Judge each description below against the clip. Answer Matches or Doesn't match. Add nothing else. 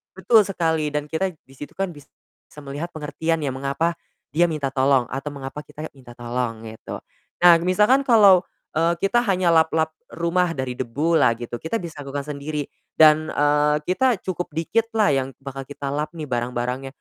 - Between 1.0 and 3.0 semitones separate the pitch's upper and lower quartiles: Doesn't match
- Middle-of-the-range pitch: Matches